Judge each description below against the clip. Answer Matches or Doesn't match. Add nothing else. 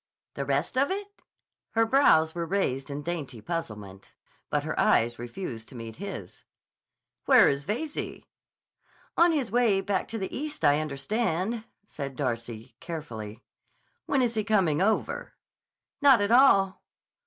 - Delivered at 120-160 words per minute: Matches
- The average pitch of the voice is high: Doesn't match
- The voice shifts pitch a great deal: Matches